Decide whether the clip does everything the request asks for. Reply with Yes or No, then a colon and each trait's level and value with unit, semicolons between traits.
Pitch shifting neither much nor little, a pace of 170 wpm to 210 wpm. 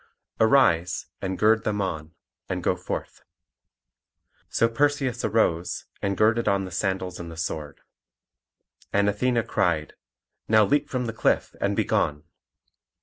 No: average, 4.8 semitones; average, 140 wpm